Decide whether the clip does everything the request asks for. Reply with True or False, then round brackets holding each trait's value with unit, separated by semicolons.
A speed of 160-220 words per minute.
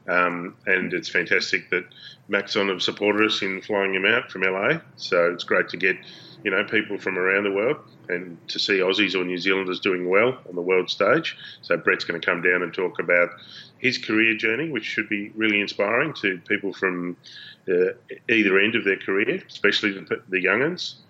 True (200 wpm)